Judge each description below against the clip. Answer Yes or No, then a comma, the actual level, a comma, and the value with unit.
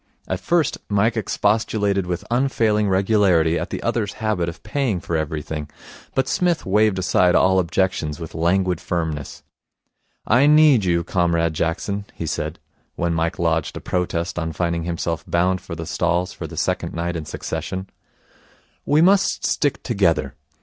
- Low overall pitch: Yes, very low, 90 Hz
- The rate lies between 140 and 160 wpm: Yes, average, 155 wpm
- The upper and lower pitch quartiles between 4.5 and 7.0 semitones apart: No, average, 4.0 semitones